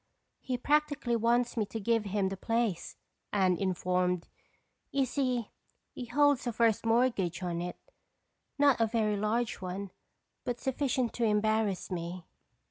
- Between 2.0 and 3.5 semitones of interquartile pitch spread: No, average, 4.3 semitones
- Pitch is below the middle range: No, high, 225 Hz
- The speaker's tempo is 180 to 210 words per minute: No, slow, 135 wpm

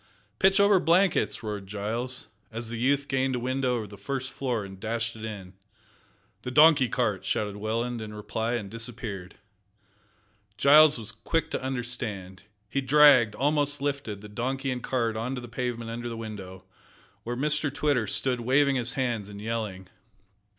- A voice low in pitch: Yes, low, 120 Hz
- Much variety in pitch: No, average, 3.8 semitones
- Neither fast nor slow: Yes, average, 165 wpm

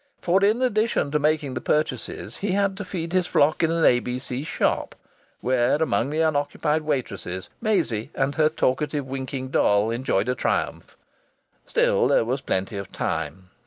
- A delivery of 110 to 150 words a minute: No, average, 165 wpm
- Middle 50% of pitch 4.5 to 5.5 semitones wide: Yes, average, 4.9 semitones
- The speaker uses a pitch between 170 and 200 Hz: No, medium, 145 Hz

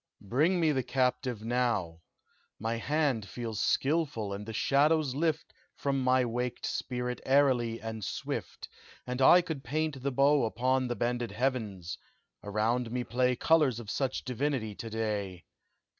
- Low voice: Yes, low, 125 Hz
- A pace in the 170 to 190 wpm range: No, average, 145 wpm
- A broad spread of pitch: No, average, 3.5 semitones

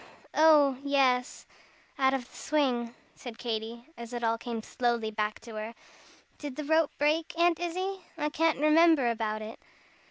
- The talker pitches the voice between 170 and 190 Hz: No, very high, 260 Hz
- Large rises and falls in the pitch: No, average, 4.8 semitones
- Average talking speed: Yes, average, 160 wpm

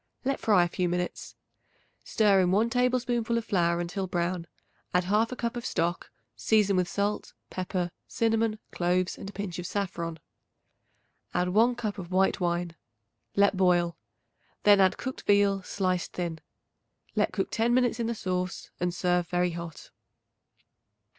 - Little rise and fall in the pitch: No, average, 3.6 semitones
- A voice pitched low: No, high, 190 Hz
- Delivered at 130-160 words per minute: Yes, average, 155 wpm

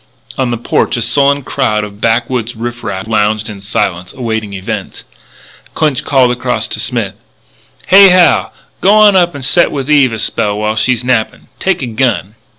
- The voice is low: Yes, low, 120 Hz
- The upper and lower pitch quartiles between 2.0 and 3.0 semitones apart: No, average, 4.6 semitones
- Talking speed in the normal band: Yes, average, 170 wpm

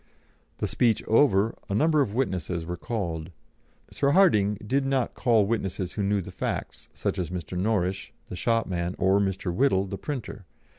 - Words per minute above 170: No, average, 165 wpm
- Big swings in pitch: No, average, 4.6 semitones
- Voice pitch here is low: Yes, low, 100 Hz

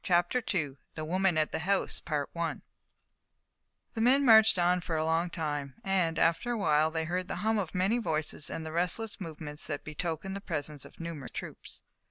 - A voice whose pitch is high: No, medium, 170 Hz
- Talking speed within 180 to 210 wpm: Yes, average, 185 wpm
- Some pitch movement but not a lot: Yes, average, 3.6 semitones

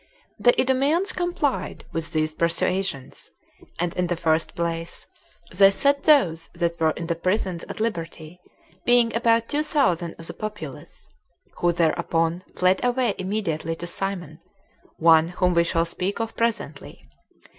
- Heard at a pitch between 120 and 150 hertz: No, medium, 180 Hz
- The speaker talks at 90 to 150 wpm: Yes, average, 145 wpm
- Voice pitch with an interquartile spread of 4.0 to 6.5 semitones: Yes, wide, 5.6 semitones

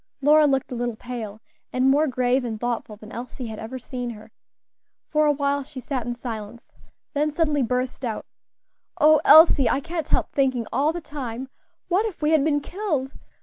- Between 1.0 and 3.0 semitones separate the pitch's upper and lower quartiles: No, average, 3.8 semitones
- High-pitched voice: Yes, very high, 265 Hz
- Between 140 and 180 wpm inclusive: No, average, 190 wpm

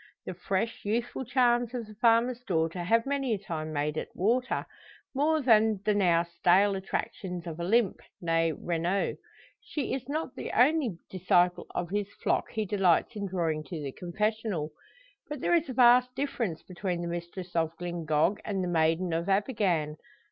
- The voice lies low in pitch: No, high, 195 Hz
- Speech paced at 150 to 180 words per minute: Yes, average, 170 wpm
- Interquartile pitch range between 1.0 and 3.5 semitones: No, wide, 5.5 semitones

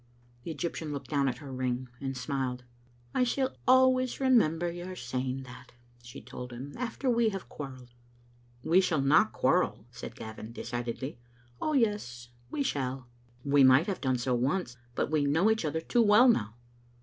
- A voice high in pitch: No, medium, 140 Hz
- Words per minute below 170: No, average, 175 wpm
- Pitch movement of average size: No, wide, 7.3 semitones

